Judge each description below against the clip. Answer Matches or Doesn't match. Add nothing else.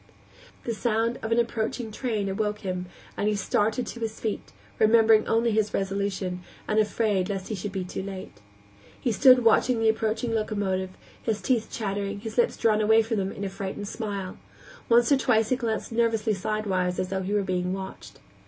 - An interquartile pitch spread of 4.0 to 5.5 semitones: Doesn't match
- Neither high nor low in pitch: Doesn't match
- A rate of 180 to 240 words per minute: Matches